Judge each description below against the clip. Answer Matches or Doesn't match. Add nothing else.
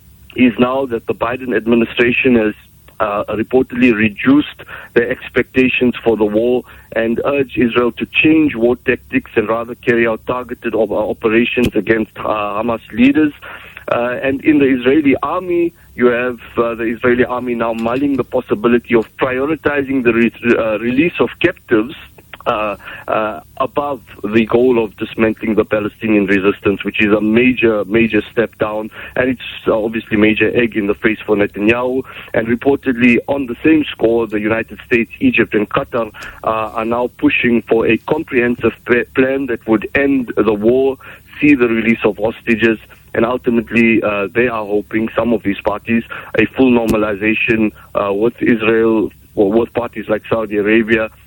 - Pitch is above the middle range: Doesn't match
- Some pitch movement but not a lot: Doesn't match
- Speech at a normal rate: Matches